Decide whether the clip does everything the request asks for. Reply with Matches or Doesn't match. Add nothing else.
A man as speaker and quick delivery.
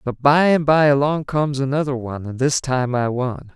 Matches